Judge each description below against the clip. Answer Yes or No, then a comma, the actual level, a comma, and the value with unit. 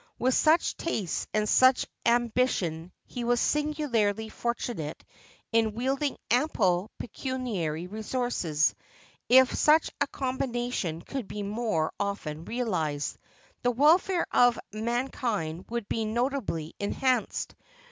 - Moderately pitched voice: No, high, 235 Hz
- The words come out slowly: Yes, slow, 115 wpm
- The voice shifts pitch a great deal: No, average, 4.8 semitones